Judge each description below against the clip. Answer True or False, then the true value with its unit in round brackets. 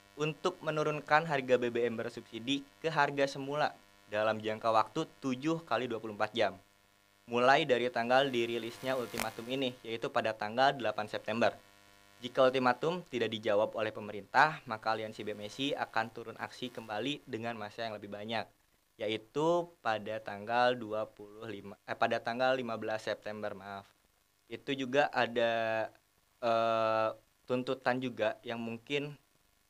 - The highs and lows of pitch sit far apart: False (3.5 semitones)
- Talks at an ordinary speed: True (125 wpm)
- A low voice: True (115 Hz)